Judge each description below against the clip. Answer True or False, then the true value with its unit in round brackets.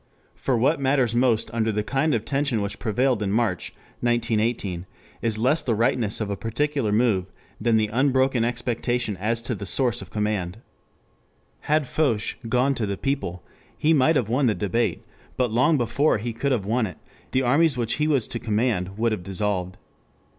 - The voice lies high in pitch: False (115 Hz)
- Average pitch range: True (3.7 semitones)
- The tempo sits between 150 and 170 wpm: False (180 wpm)